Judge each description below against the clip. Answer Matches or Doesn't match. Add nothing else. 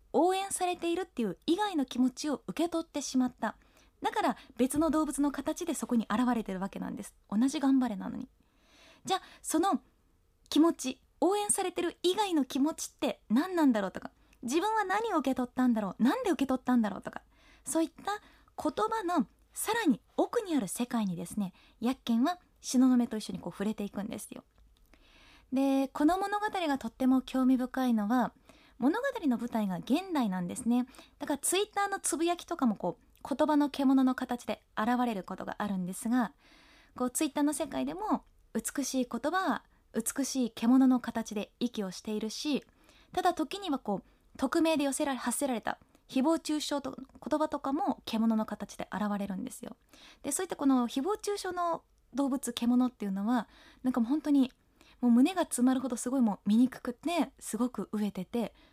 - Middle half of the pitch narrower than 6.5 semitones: Matches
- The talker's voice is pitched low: Doesn't match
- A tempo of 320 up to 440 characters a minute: Matches